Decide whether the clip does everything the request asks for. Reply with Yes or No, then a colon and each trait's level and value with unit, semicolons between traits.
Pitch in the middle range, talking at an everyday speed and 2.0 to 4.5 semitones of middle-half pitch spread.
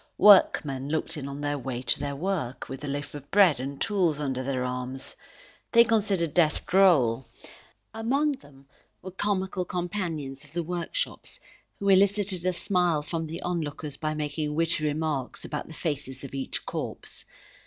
No: medium, 155 Hz; average, 165 wpm; average, 5.0 semitones